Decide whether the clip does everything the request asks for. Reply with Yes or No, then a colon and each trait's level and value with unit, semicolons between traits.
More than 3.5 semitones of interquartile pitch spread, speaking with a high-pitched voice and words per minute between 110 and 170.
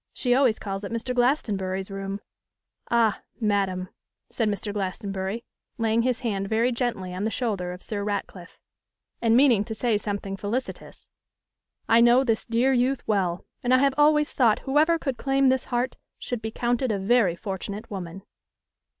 Yes: average, 4.1 semitones; high, 225 Hz; average, 165 wpm